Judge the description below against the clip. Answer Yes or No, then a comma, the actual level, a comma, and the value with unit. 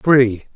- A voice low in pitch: Yes, low, 125 Hz